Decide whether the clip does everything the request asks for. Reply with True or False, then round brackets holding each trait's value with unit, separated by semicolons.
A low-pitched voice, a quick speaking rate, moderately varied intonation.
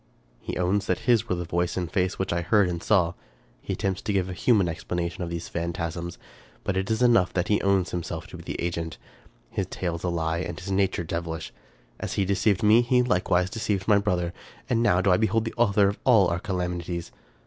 True (90 Hz; 225 wpm; 3.0 semitones)